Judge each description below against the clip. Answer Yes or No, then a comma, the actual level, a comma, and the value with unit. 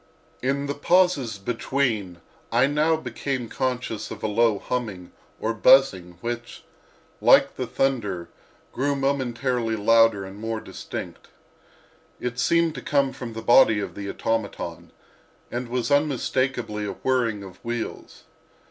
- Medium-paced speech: No, slow, 130 wpm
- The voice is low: Yes, low, 120 Hz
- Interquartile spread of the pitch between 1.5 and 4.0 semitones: Yes, average, 3.7 semitones